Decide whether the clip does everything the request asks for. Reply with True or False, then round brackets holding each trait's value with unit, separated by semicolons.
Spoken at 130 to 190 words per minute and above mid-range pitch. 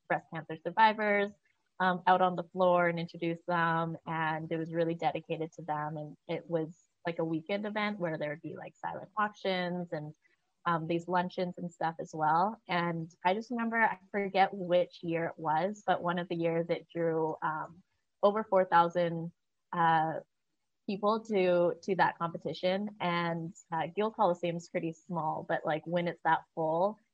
False (175 wpm; 175 Hz)